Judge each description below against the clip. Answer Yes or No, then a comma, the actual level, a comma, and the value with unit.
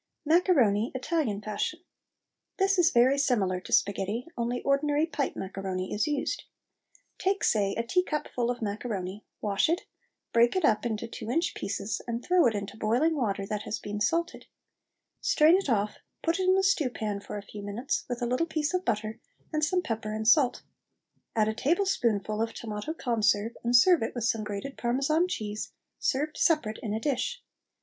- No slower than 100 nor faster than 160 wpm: No, average, 180 wpm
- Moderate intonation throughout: No, wide, 6.4 semitones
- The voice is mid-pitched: No, high, 235 Hz